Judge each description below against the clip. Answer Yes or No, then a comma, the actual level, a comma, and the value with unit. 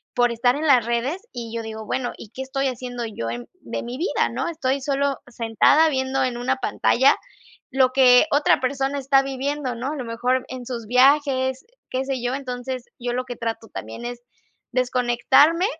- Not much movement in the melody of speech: Yes, narrow, 2.1 semitones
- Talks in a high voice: Yes, very high, 255 Hz